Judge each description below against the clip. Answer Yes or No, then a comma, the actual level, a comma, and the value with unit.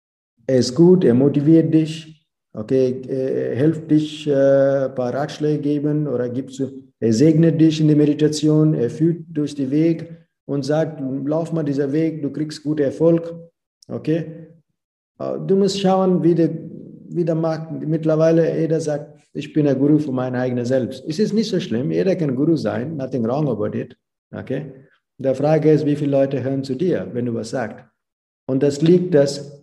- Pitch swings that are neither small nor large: Yes, average, 3.1 semitones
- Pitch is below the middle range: No, medium, 150 Hz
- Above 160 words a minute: Yes, average, 185 wpm